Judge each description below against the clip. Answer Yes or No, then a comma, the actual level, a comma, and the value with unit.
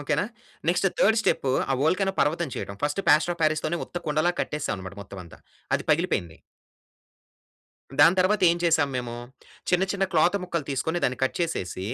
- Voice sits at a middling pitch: Yes, medium, 155 Hz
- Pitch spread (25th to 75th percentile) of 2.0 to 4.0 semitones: No, average, 4.5 semitones